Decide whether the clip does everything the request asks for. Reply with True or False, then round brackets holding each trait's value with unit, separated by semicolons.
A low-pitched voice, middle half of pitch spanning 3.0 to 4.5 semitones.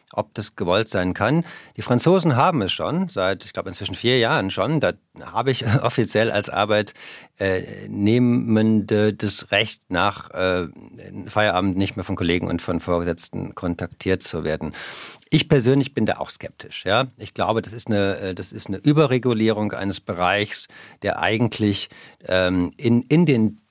True (105 Hz; 4.1 semitones)